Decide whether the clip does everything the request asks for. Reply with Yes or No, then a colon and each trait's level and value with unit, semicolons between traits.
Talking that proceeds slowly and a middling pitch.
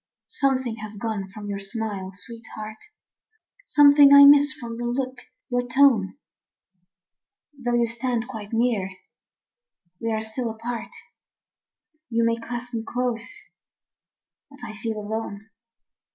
No: slow, 125 wpm; high, 230 Hz